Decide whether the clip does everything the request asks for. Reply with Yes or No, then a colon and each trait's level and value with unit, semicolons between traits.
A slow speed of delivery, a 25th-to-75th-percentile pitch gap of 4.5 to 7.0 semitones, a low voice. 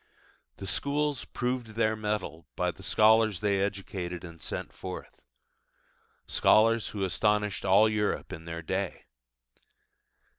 No: slow, 120 wpm; average, 2.8 semitones; low, 105 Hz